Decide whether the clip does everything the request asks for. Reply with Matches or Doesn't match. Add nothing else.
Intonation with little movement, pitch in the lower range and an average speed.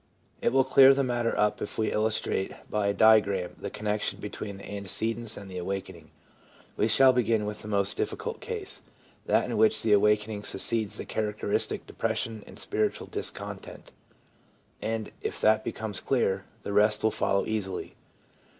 Matches